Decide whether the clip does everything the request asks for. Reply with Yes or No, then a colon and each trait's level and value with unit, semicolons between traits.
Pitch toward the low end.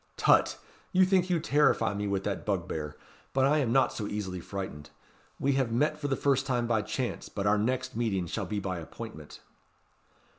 Yes: low, 115 Hz